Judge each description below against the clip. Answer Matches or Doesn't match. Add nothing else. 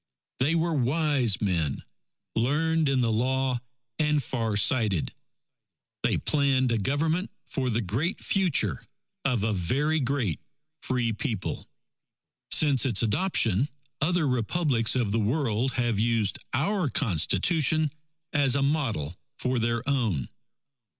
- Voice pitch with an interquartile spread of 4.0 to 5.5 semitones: Matches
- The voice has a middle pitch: Doesn't match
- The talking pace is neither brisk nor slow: Doesn't match